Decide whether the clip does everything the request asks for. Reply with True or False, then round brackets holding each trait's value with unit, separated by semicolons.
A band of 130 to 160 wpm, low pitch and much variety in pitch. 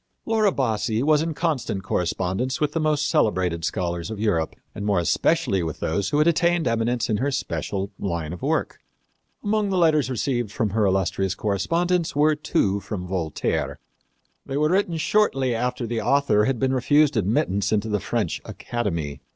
False (170 wpm; 115 Hz; 7.5 semitones)